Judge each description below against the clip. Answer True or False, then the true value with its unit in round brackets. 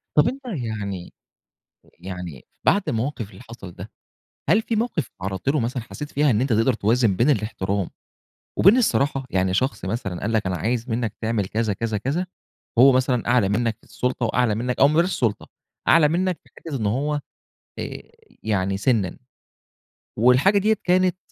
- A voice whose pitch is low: True (120 Hz)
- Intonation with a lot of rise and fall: True (5.8 semitones)